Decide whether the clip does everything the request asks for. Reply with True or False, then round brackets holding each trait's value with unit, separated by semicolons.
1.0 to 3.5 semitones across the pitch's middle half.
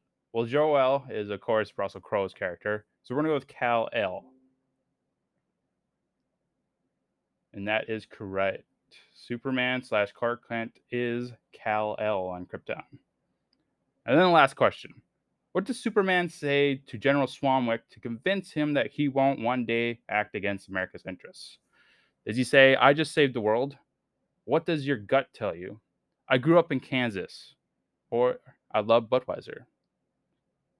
False (4.3 semitones)